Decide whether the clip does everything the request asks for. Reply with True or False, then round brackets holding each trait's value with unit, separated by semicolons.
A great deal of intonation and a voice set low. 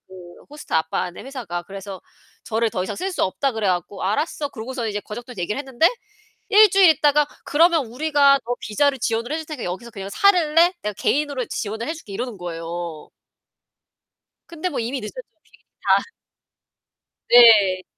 False (7.1 semitones; 240 Hz)